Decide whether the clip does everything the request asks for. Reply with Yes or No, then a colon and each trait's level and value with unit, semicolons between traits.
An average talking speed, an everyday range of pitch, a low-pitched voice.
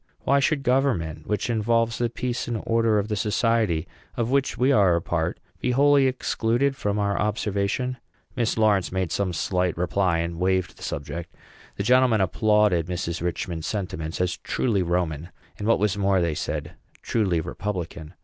Yes: average, 170 wpm; average, 4.9 semitones; low, 100 Hz